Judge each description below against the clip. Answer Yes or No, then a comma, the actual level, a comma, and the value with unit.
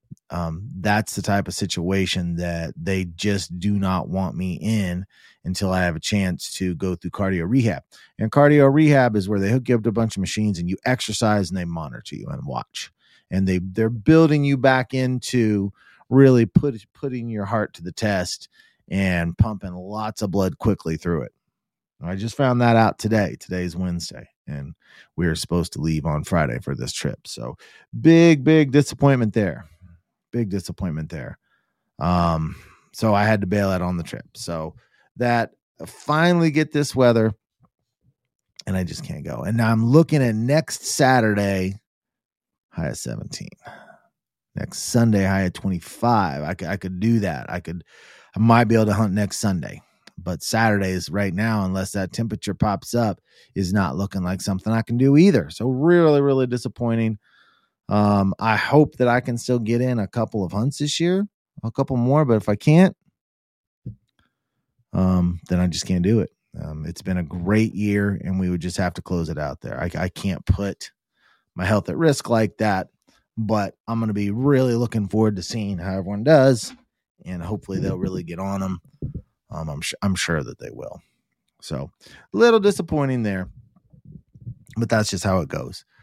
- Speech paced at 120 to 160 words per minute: No, average, 185 wpm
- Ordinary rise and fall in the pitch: Yes, average, 4.6 semitones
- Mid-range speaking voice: No, low, 105 Hz